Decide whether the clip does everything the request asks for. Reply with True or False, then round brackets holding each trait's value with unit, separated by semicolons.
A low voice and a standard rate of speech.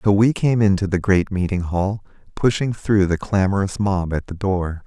True (95 Hz; 195 wpm)